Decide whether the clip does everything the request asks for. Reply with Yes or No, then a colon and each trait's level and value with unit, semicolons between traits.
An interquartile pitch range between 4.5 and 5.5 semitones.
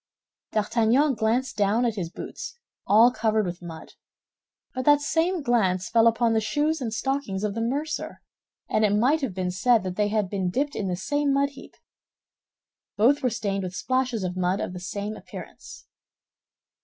Yes: average, 5.1 semitones